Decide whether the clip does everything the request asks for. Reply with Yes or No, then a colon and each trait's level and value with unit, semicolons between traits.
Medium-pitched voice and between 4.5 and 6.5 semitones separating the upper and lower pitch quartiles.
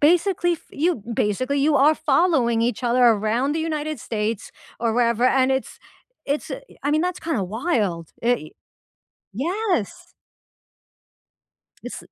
No: very high, 265 Hz; wide, 5.6 semitones